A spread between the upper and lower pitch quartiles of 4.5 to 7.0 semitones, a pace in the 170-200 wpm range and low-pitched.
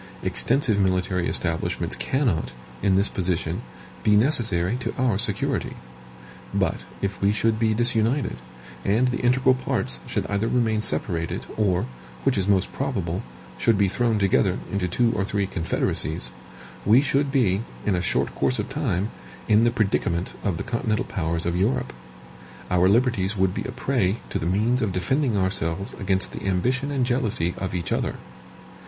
No: average, 4.8 semitones; average, 160 wpm; low, 100 Hz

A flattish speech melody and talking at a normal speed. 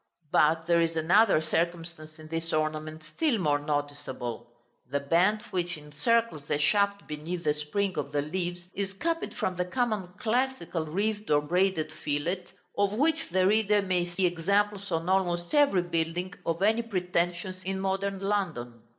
No: average, 4.3 semitones; average, 160 wpm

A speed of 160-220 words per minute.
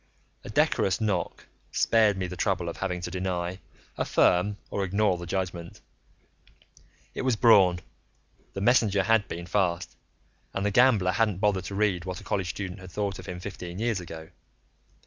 Yes: average, 165 wpm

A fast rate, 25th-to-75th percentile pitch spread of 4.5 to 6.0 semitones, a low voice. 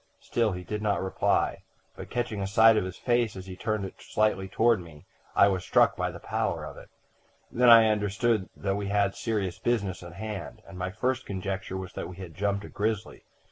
No: fast, 215 wpm; narrow, 2.6 semitones; low, 100 Hz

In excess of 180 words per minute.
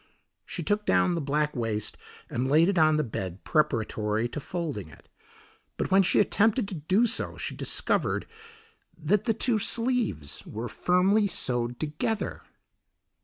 No: average, 150 wpm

